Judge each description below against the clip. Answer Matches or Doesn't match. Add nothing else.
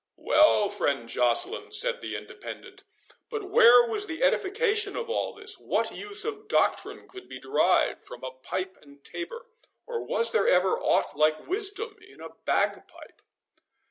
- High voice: Matches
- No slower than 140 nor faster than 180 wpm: Matches